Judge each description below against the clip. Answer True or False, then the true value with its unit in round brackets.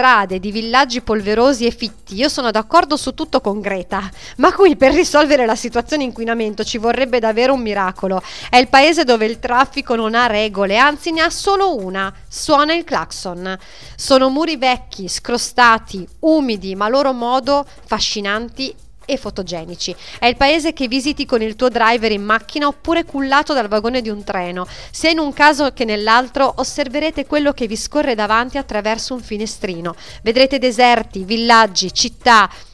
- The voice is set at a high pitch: True (245 Hz)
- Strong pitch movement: False (4.5 semitones)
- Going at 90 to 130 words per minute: False (165 wpm)